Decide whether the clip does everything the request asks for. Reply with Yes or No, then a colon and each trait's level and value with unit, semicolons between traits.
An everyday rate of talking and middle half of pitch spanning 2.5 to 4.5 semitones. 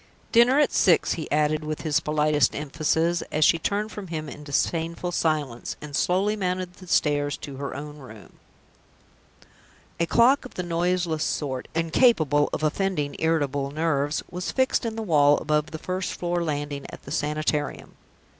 Yes: average, 165 wpm; average, 3.4 semitones